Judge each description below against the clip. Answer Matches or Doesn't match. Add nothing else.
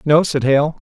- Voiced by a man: Matches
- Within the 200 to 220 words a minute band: Matches